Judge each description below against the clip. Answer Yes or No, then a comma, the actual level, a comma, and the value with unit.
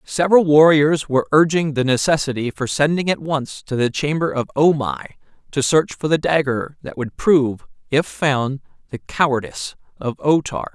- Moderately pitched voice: Yes, medium, 145 Hz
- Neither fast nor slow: Yes, average, 175 wpm